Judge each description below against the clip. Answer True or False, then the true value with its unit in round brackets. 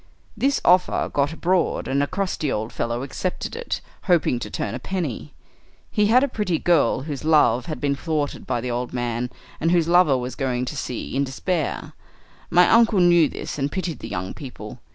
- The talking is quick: False (195 wpm)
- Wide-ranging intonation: True (6.0 semitones)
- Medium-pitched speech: True (150 Hz)